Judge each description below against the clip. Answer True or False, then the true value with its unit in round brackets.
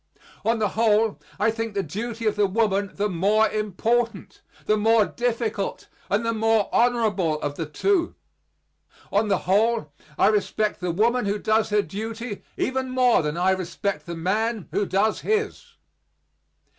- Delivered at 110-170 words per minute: True (155 wpm)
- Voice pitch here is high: True (215 Hz)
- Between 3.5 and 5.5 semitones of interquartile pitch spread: False (2.6 semitones)